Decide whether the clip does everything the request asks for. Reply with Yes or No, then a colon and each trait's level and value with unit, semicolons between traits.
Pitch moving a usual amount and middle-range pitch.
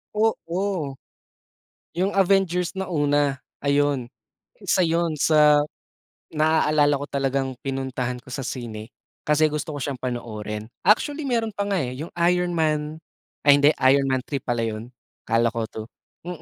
Yes: average, 4.8 semitones; medium, 145 Hz